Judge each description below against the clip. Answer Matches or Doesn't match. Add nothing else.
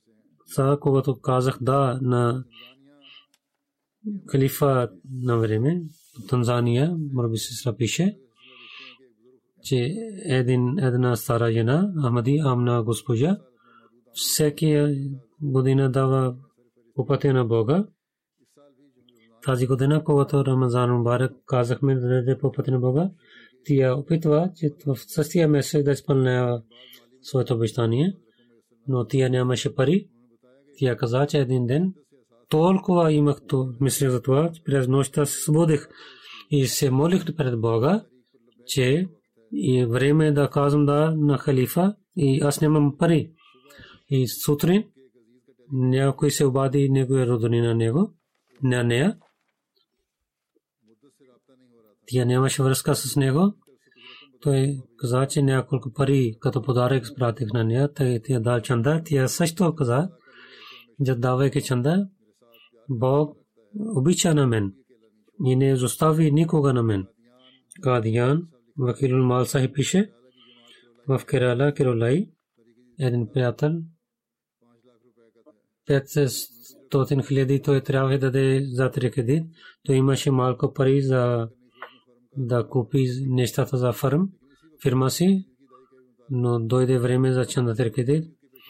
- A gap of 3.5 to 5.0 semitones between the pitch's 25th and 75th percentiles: Doesn't match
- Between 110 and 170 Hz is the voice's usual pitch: Matches